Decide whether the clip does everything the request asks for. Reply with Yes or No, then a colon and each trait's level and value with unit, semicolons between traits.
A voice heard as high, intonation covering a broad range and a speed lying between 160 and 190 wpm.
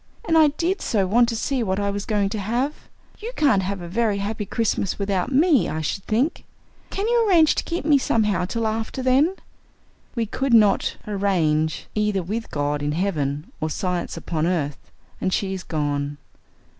Yes: high, 205 Hz; wide, 5.9 semitones; average, 185 wpm